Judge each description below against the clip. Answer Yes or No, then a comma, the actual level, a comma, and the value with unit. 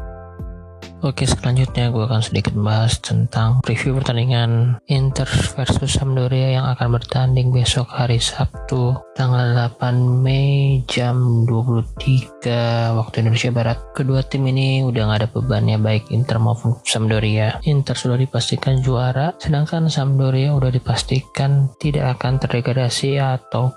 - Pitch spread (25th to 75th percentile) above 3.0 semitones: No, narrow, 2.4 semitones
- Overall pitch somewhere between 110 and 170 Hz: Yes, low, 125 Hz